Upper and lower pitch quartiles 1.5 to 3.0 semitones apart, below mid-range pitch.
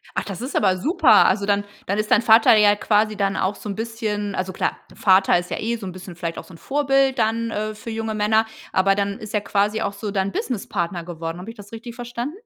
No: narrow, 2.5 semitones; high, 210 Hz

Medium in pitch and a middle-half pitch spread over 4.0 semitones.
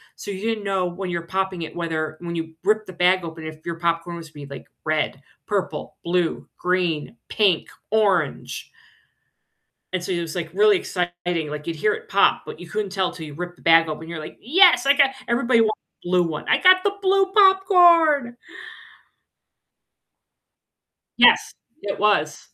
Yes: medium, 180 Hz; average, 4.5 semitones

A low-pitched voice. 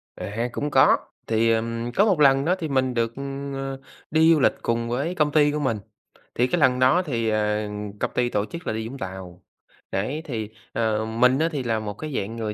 Yes: low, 120 Hz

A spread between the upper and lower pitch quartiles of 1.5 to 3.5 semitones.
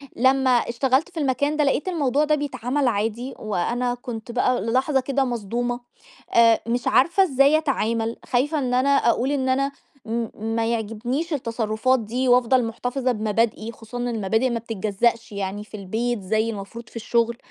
Yes: average, 2.8 semitones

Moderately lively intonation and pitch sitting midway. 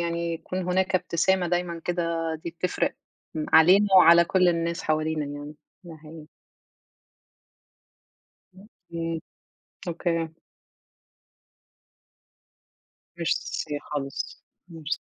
No: narrow, 1.8 semitones; medium, 170 Hz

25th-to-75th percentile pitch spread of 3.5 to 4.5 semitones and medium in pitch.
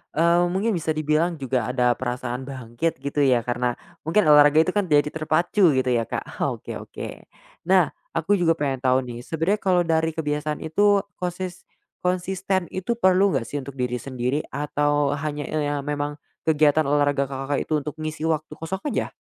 Yes: average, 3.9 semitones; medium, 150 Hz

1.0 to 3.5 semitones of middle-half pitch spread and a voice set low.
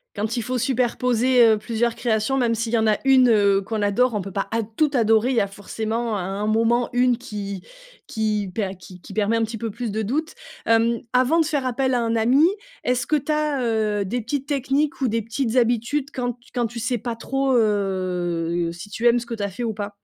No: average, 3.0 semitones; high, 230 Hz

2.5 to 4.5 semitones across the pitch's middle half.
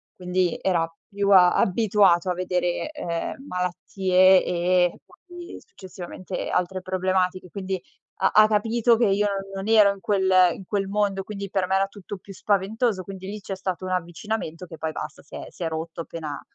No: narrow, 2.0 semitones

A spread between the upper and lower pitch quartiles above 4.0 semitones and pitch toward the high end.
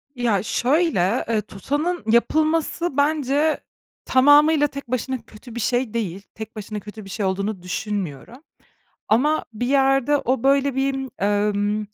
Yes: average, 5.1 semitones; high, 245 Hz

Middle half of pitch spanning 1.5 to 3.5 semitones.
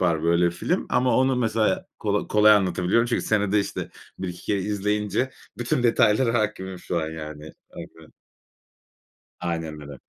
No: average, 4.7 semitones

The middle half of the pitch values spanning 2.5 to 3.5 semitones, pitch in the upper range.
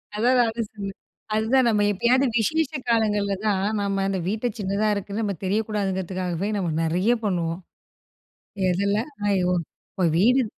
Yes: average, 2.8 semitones; high, 205 Hz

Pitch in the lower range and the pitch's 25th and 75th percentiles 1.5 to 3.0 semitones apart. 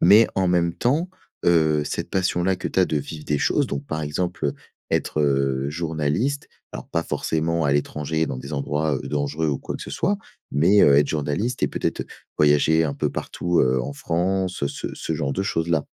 No: very low, 80 Hz; average, 3.6 semitones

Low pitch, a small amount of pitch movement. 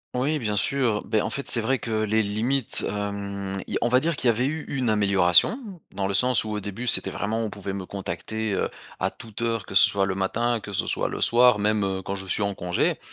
No: low, 105 Hz; average, 3.4 semitones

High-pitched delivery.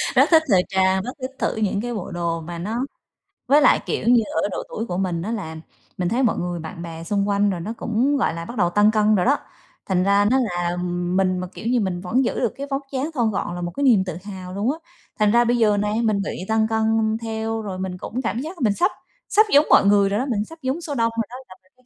Yes: high, 210 Hz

